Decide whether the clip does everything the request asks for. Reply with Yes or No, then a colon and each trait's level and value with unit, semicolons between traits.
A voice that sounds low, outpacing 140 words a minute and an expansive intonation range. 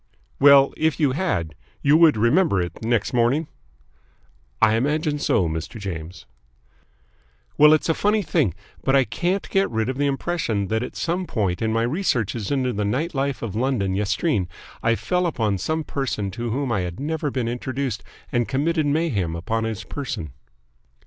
Yes: low, 125 Hz; average, 170 wpm; wide, 6.2 semitones